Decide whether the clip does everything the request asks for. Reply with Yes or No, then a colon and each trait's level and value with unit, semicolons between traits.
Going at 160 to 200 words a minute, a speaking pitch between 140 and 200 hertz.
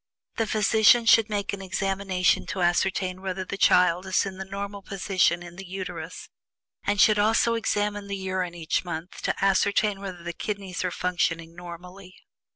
Yes: average, 165 wpm; high, 190 Hz